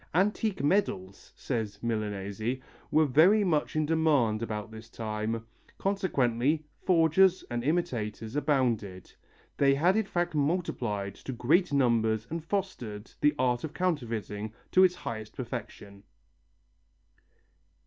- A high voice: No, low, 130 Hz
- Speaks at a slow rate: Yes, slow, 120 wpm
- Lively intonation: Yes, wide, 6.9 semitones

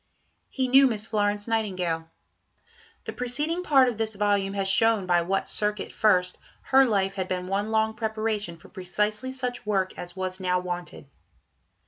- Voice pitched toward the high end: Yes, high, 210 Hz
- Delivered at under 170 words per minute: Yes, average, 160 wpm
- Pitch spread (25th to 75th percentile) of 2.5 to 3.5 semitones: Yes, average, 3.2 semitones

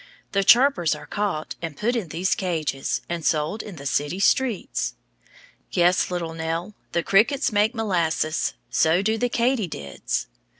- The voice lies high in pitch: No, medium, 180 Hz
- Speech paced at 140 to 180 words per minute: Yes, average, 145 wpm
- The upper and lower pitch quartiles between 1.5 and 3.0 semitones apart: No, average, 5.0 semitones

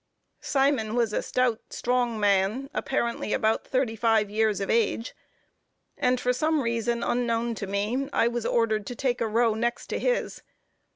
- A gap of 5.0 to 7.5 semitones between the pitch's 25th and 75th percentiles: No, narrow, 2.4 semitones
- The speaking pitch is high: Yes, high, 235 Hz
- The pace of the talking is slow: No, average, 165 wpm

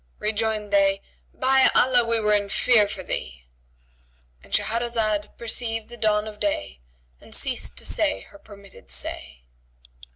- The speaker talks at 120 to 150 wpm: Yes, slow, 135 wpm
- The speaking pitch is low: No, high, 205 Hz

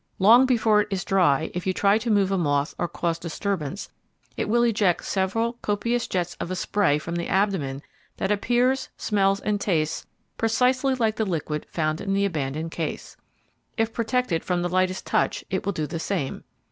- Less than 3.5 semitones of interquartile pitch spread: No, average, 4.5 semitones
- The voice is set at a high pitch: Yes, high, 195 Hz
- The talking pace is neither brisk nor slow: Yes, average, 185 wpm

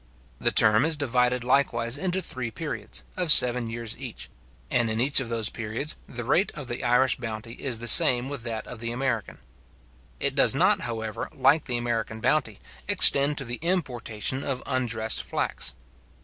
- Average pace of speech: Yes, average, 175 wpm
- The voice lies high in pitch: No, low, 120 Hz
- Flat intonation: No, average, 3.1 semitones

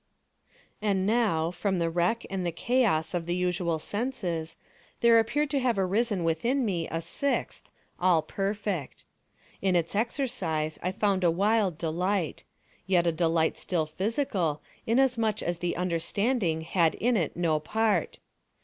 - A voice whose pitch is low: No, medium, 185 Hz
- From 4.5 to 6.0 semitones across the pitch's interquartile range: Yes, average, 4.9 semitones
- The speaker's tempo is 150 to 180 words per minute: No, average, 140 wpm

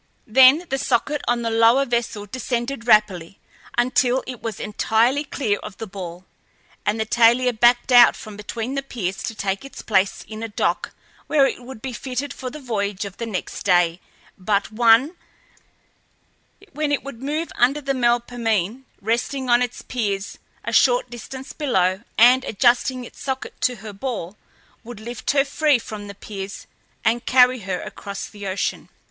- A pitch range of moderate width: Yes, average, 3.8 semitones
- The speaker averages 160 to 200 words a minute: Yes, average, 170 wpm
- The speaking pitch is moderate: No, high, 235 Hz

